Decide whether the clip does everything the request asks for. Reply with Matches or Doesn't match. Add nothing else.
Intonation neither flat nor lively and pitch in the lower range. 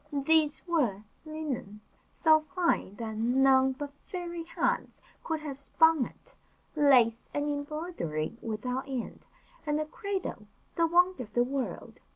Doesn't match